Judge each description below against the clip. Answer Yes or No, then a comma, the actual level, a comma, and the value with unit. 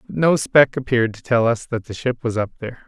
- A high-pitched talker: No, low, 120 Hz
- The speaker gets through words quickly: Yes, fast, 270 wpm